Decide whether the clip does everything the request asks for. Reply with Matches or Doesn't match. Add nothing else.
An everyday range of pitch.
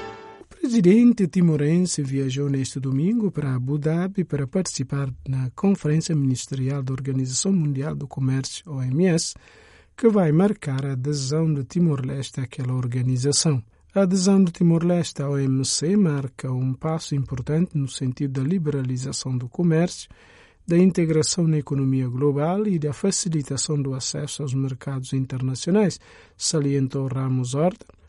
Matches